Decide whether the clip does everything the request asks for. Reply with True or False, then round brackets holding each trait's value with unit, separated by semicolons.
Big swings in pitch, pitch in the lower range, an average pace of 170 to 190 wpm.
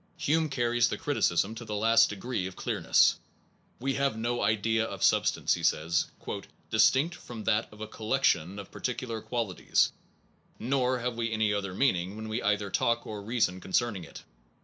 False (2.9 semitones; 110 Hz; 175 wpm)